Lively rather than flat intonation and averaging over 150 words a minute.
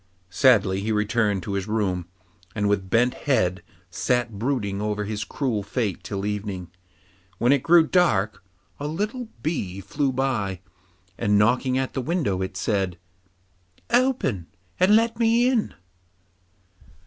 No: wide, 6.2 semitones; slow, 135 wpm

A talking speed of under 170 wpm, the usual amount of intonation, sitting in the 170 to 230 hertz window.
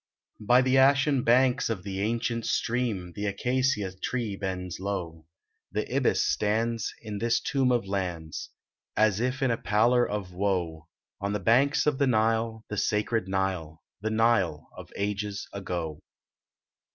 No: average, 150 wpm; average, 3.9 semitones; low, 105 Hz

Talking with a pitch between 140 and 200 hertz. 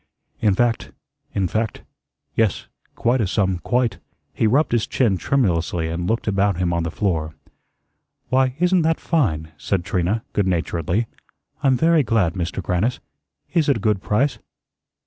No: low, 105 Hz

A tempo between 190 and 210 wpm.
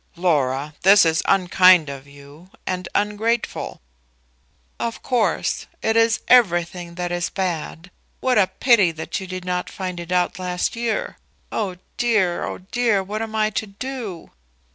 No: average, 150 wpm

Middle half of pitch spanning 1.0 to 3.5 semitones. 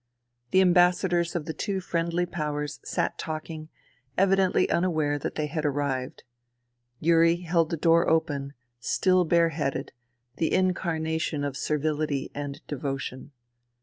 Yes: average, 2.9 semitones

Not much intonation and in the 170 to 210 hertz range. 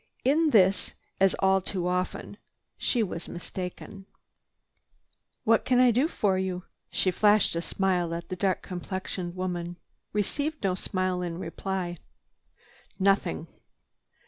Yes: narrow, 2.2 semitones; high, 190 Hz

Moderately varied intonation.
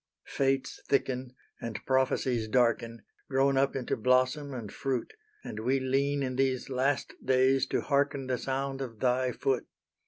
No: narrow, 1.3 semitones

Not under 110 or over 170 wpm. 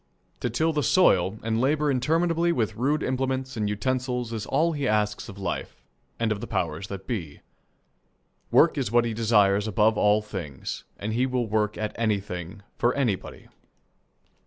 Yes: average, 165 wpm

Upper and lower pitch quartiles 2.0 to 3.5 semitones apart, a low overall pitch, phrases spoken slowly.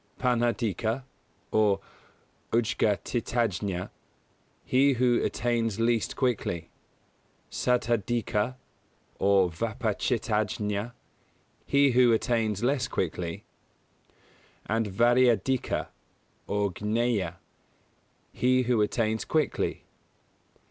Yes: average, 2.9 semitones; low, 115 Hz; slow, 70 wpm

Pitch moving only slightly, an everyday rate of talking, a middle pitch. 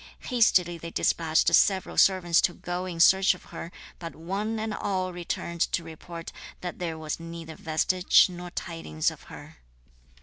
Yes: narrow, 1.9 semitones; average, 160 wpm; medium, 175 Hz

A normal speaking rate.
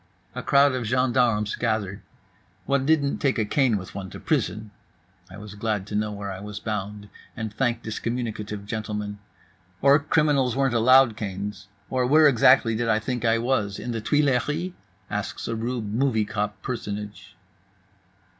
Yes: average, 165 wpm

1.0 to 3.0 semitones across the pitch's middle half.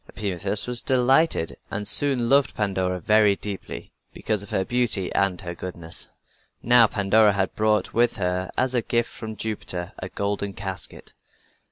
No: average, 3.8 semitones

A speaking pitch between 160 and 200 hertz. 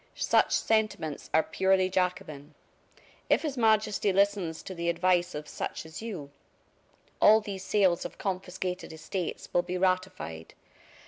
Yes: medium, 185 Hz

